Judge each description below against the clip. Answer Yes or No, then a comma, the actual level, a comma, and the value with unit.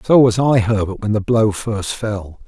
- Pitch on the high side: No, low, 110 Hz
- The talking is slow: No, fast, 220 wpm